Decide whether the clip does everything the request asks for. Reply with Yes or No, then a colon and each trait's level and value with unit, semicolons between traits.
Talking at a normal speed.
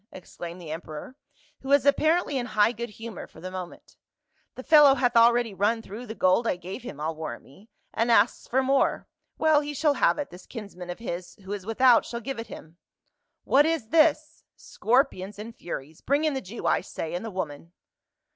No: fast, 215 wpm